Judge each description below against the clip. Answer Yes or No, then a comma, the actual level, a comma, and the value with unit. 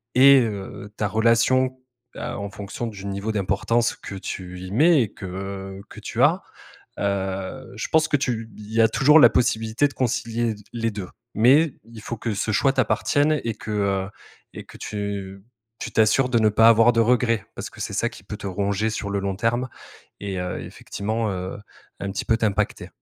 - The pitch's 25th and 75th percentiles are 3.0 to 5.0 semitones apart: Yes, average, 3.3 semitones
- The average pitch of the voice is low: Yes, low, 110 Hz